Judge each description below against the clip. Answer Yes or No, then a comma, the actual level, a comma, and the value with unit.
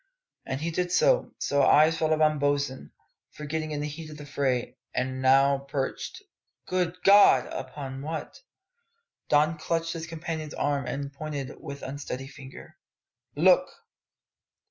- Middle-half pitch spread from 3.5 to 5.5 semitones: No, average, 2.7 semitones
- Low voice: No, medium, 145 Hz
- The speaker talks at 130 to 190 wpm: Yes, average, 140 wpm